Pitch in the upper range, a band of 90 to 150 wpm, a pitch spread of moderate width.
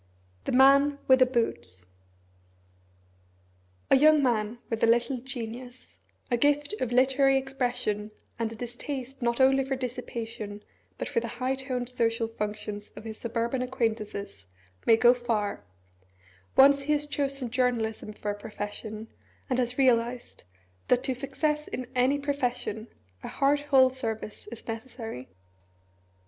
Yes: high, 245 Hz; average, 140 wpm; average, 3.1 semitones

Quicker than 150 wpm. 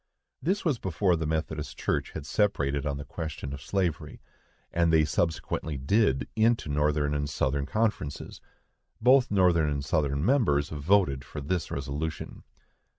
No: average, 145 wpm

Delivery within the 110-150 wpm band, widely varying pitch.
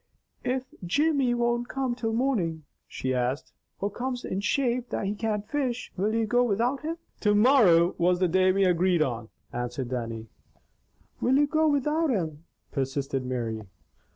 No: average, 160 wpm; wide, 8.0 semitones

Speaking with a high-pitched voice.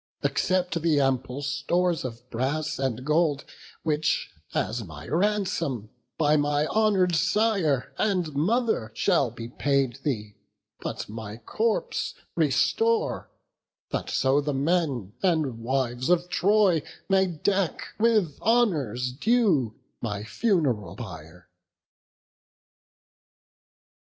No: medium, 145 Hz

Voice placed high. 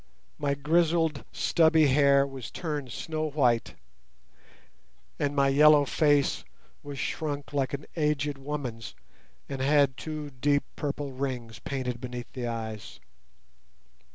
No: medium, 140 Hz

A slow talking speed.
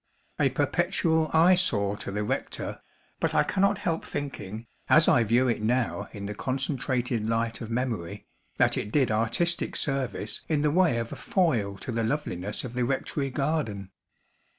No: average, 165 wpm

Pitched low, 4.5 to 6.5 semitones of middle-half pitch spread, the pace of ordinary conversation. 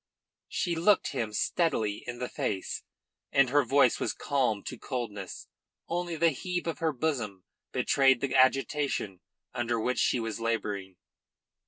Yes: low, 125 Hz; average, 5.1 semitones; average, 145 wpm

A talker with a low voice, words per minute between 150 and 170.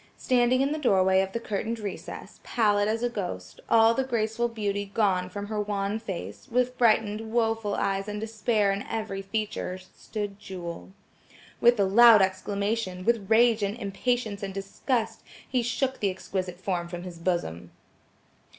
No: high, 210 Hz; average, 160 wpm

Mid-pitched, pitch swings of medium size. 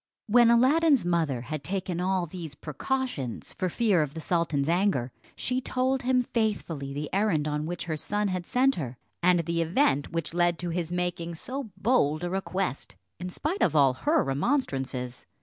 No: medium, 175 Hz; wide, 6.9 semitones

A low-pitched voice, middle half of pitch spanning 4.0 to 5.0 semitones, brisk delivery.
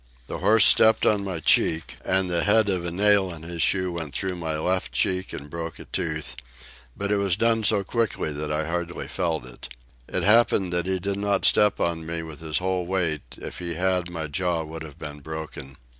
No: very low, 85 Hz; average, 3.4 semitones; fast, 215 wpm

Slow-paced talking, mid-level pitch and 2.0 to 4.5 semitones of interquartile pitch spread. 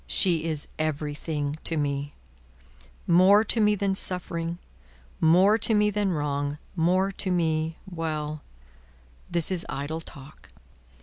Yes: slow, 125 wpm; medium, 165 Hz; average, 3.8 semitones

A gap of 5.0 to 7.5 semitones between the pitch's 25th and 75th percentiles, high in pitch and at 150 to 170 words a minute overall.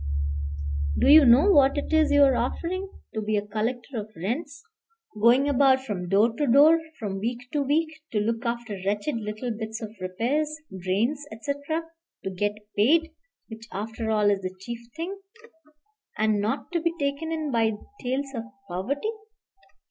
Yes: average, 5.3 semitones; high, 240 Hz; average, 165 wpm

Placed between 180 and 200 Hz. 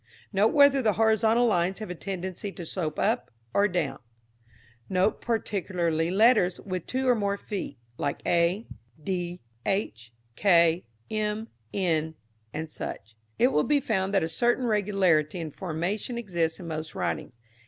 Yes: high, 190 Hz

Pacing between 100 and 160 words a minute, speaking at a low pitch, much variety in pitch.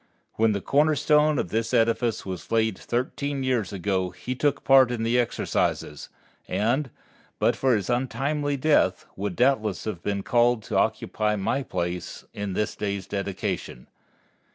No: average, 155 wpm; low, 115 Hz; average, 4.7 semitones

